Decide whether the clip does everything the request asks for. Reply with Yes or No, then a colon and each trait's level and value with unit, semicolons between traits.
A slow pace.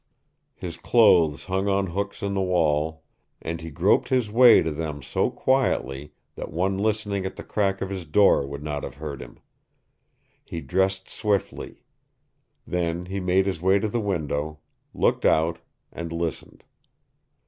No: average, 160 wpm